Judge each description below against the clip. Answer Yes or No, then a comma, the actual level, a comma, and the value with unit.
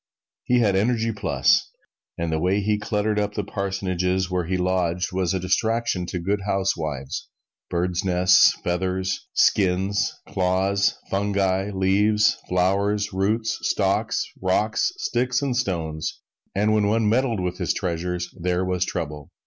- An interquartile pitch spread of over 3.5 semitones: No, narrow, 2.4 semitones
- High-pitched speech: No, very low, 95 Hz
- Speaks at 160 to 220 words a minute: No, average, 140 wpm